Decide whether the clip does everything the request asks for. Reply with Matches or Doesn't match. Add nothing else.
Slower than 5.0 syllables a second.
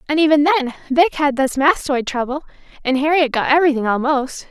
Doesn't match